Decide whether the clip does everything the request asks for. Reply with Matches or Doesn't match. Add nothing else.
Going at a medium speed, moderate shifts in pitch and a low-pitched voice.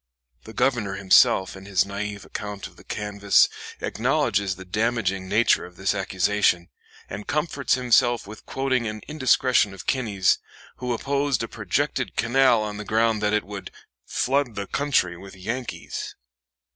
Matches